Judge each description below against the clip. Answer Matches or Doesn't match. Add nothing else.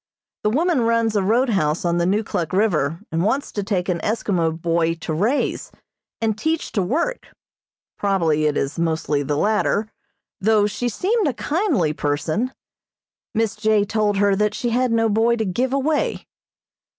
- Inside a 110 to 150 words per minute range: Doesn't match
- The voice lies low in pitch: Doesn't match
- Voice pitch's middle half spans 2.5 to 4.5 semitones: Doesn't match